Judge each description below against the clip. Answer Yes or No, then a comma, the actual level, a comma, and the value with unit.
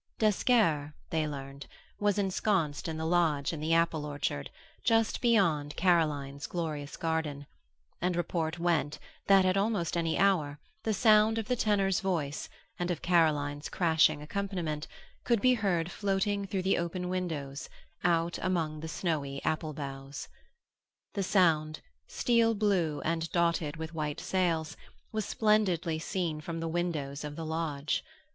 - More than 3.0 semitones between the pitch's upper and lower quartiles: Yes, average, 4.0 semitones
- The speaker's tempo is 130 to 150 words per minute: Yes, average, 145 wpm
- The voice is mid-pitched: Yes, medium, 165 Hz